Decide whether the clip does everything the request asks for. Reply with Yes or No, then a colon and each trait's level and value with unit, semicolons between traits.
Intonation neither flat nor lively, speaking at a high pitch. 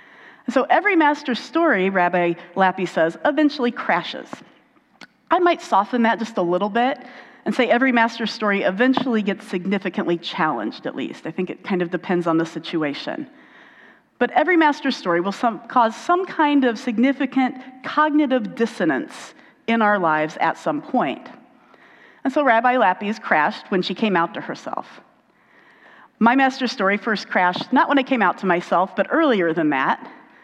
No: wide, 6.5 semitones; high, 240 Hz